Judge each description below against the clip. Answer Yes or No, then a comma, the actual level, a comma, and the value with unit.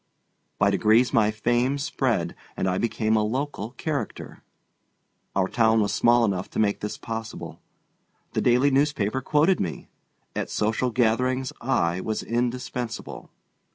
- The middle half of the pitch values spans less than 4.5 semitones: Yes, average, 3.2 semitones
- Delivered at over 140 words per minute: No, slow, 135 wpm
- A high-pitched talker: No, low, 115 Hz